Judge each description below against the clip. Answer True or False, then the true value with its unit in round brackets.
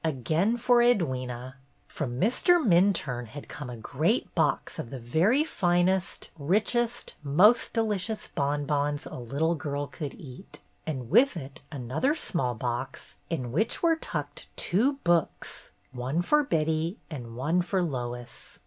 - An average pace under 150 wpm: True (140 wpm)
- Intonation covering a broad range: True (7.5 semitones)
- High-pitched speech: False (155 Hz)